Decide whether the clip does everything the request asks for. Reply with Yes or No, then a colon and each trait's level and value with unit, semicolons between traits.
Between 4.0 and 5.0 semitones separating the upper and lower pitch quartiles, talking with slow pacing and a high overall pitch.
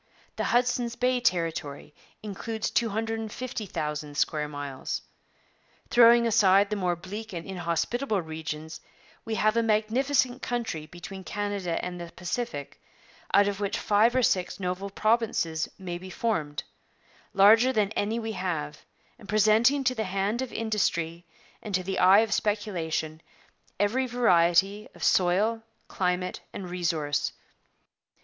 Yes: average, 4.5 semitones; slow, 130 wpm; high, 200 Hz